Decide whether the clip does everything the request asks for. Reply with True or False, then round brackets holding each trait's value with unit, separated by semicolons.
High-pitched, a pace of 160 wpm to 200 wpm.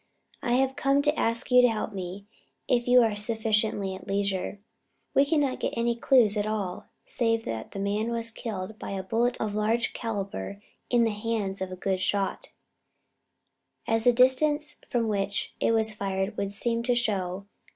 True (220 Hz; 180 wpm)